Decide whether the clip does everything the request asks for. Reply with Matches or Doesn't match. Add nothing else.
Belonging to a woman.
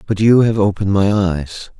Doesn't match